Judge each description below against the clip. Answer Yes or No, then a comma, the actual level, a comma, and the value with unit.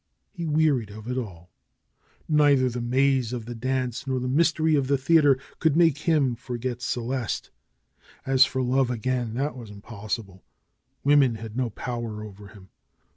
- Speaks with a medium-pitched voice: No, low, 125 Hz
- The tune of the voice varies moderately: Yes, average, 3.3 semitones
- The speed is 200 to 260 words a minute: No, average, 160 wpm